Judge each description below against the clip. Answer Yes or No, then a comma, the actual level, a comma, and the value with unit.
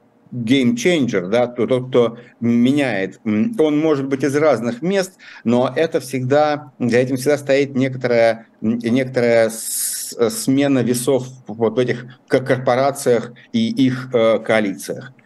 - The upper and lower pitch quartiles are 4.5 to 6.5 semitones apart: No, average, 2.7 semitones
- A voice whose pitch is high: No, low, 125 Hz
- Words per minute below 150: Yes, average, 115 wpm